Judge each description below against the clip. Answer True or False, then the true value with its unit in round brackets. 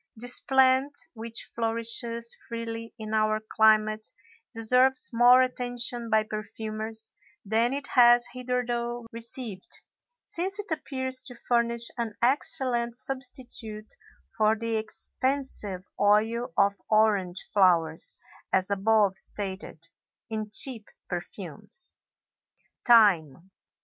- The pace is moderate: False (100 wpm)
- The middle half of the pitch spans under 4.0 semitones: True (2.4 semitones)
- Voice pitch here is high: True (230 Hz)